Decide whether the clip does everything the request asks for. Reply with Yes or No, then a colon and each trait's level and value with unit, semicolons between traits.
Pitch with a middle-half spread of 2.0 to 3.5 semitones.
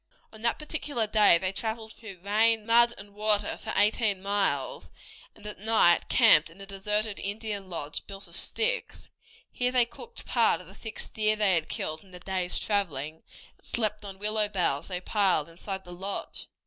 Yes: average, 2.8 semitones